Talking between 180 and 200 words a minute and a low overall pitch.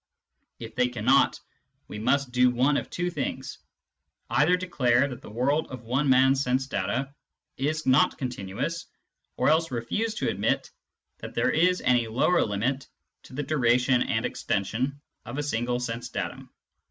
No: average, 155 wpm; low, 130 Hz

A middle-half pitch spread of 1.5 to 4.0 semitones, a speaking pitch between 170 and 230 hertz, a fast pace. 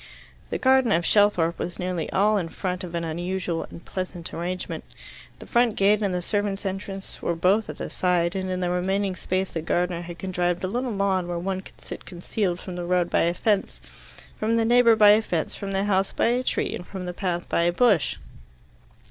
Yes: narrow, 2.6 semitones; medium, 185 Hz; fast, 215 wpm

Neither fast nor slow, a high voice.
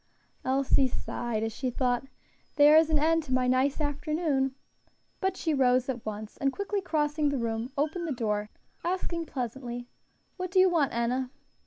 Yes: average, 170 wpm; very high, 270 Hz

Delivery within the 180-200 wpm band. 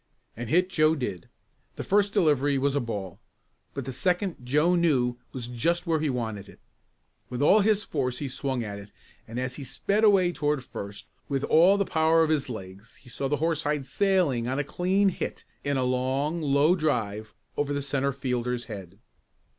Yes: average, 190 wpm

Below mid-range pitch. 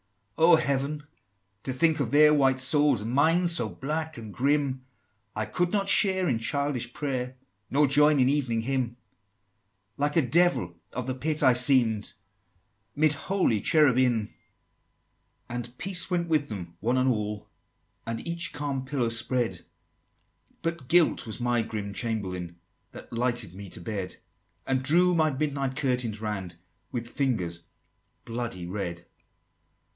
Yes: low, 130 Hz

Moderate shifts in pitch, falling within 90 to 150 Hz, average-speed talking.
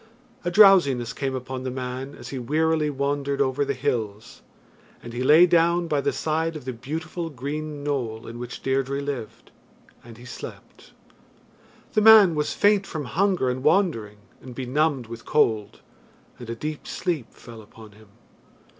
Yes: average, 4.4 semitones; medium, 140 Hz; average, 165 wpm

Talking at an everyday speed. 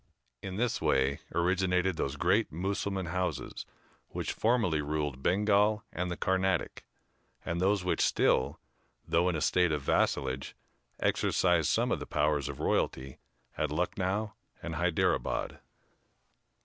No: slow, 130 wpm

